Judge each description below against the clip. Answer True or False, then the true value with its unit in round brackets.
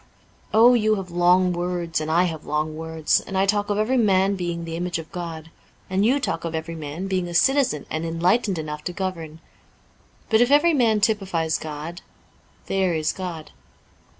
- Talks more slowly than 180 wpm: False (185 wpm)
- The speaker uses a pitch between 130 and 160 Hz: False (175 Hz)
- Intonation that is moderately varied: True (3.9 semitones)